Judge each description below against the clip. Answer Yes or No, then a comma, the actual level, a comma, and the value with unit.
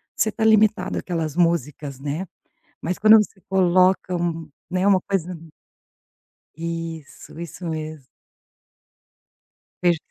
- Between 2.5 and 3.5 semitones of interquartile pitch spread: Yes, average, 2.8 semitones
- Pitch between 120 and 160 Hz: No, medium, 170 Hz